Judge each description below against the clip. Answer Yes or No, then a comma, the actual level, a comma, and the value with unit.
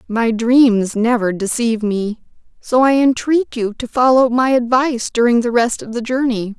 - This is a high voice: Yes, high, 240 Hz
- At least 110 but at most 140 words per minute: No, average, 175 wpm